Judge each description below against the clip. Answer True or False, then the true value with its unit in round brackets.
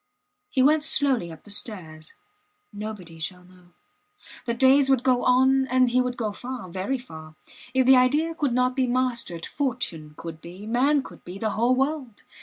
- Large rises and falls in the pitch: True (6.2 semitones)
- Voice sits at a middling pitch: False (245 Hz)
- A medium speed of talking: True (180 wpm)